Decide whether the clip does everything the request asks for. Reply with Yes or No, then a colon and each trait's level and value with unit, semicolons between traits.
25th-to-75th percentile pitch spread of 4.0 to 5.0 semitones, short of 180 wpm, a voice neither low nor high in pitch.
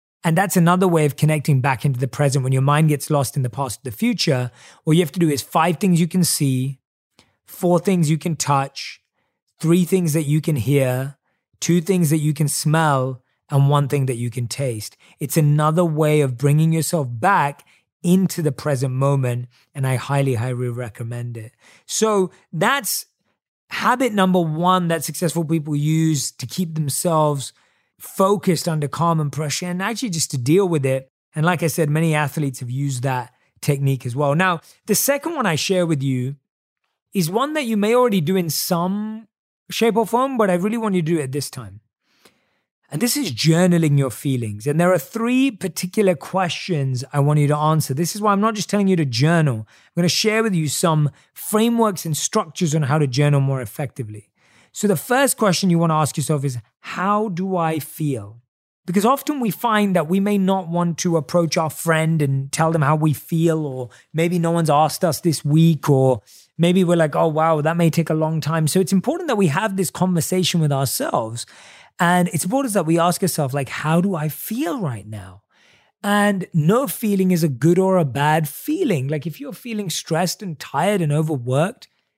No: average, 4.6 semitones; average, 200 wpm; medium, 160 Hz